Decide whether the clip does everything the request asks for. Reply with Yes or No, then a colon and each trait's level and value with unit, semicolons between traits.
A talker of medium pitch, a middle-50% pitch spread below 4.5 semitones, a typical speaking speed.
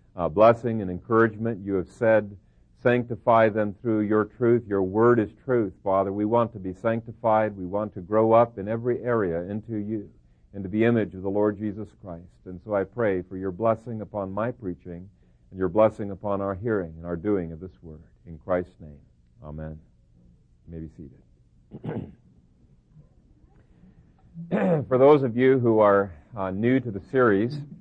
No: low, 105 Hz; average, 4.0 semitones; average, 175 wpm